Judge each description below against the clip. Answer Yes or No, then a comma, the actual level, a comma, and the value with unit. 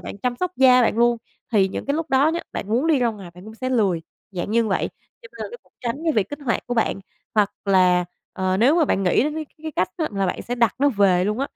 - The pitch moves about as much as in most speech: No, wide, 5.7 semitones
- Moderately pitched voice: No, high, 230 Hz